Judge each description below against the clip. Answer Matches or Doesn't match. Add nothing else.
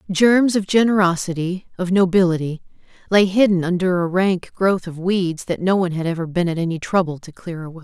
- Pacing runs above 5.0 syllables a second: Matches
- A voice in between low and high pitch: Matches